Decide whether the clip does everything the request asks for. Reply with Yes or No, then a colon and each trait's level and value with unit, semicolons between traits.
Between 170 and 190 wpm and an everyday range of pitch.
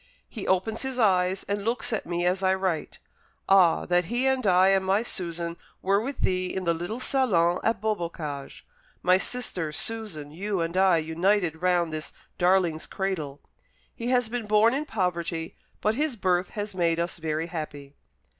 Yes: average, 175 wpm; average, 4.0 semitones